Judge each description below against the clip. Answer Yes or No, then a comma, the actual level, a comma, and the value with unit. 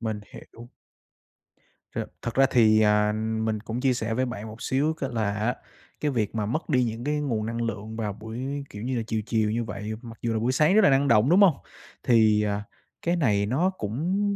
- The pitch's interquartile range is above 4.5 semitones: No, average, 3.8 semitones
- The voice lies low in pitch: Yes, low, 115 Hz